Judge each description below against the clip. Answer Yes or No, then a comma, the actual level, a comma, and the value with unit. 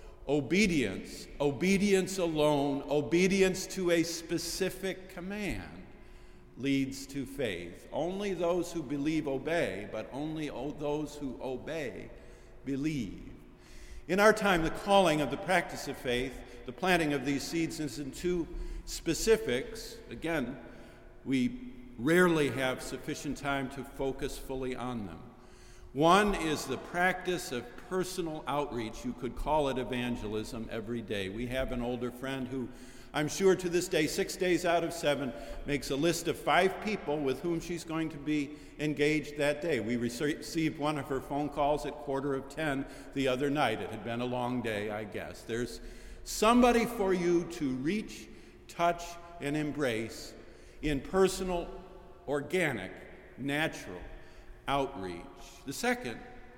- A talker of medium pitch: Yes, medium, 145 Hz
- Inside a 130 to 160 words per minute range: Yes, average, 145 wpm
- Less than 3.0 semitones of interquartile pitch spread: No, average, 5.0 semitones